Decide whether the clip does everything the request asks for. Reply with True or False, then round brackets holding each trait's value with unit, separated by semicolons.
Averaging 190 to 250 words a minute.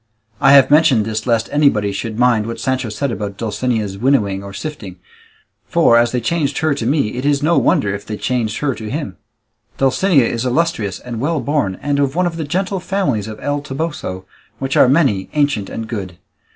True (200 wpm)